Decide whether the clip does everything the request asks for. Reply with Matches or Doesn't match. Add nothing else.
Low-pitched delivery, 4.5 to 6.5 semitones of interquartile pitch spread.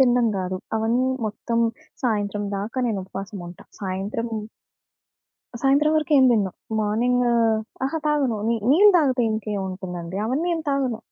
Doesn't match